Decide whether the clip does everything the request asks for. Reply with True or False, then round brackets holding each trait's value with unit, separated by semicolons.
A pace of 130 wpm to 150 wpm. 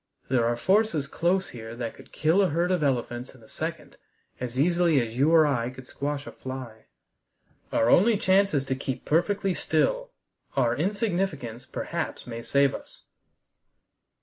False (165 wpm)